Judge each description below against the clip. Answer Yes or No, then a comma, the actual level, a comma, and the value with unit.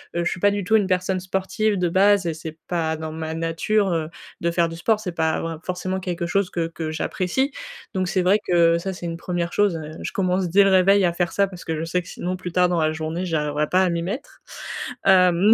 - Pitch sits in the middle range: Yes, medium, 180 Hz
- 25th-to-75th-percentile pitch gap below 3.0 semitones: Yes, narrow, 2.4 semitones